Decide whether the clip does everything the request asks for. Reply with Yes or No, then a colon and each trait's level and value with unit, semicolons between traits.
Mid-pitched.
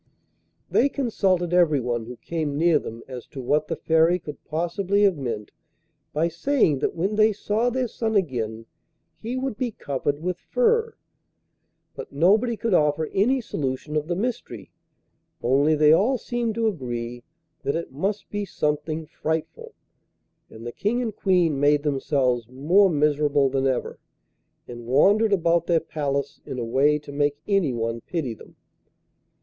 Yes: medium, 155 Hz